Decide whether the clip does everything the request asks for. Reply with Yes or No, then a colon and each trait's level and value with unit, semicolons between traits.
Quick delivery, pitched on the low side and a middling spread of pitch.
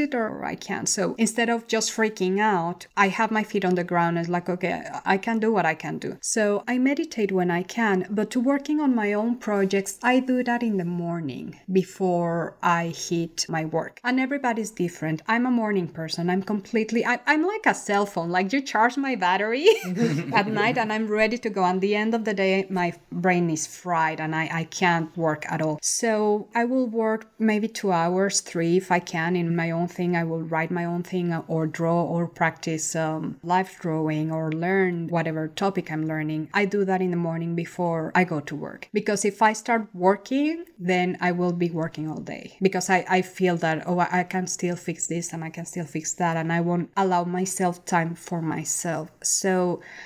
No: fast, 210 wpm; medium, 180 Hz; average, 4.2 semitones